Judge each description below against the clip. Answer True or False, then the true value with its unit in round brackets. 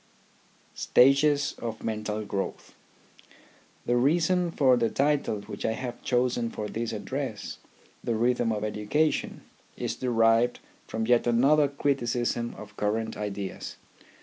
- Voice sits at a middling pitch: False (120 Hz)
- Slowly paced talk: True (120 wpm)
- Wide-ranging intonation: False (3.6 semitones)